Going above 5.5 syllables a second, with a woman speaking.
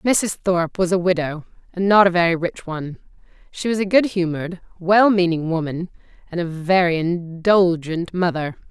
No: 5.0 syllables/s; female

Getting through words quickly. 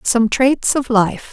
No: average, 180 wpm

